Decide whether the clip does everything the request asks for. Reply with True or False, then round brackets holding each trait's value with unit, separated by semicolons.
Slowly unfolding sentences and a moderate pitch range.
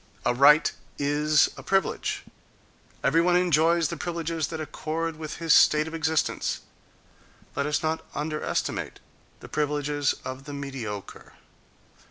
False (130 wpm; 2.0 semitones)